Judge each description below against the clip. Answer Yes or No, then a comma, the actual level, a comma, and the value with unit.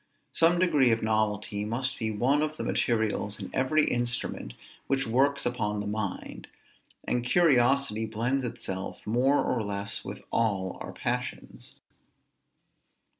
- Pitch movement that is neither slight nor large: Yes, average, 4.2 semitones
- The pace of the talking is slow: Yes, slow, 130 wpm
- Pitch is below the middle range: Yes, low, 115 Hz